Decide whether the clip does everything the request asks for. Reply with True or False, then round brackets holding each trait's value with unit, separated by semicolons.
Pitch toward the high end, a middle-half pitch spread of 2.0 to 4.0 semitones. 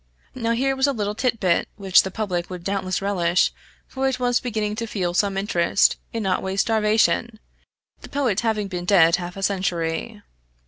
True (205 Hz; 3.7 semitones)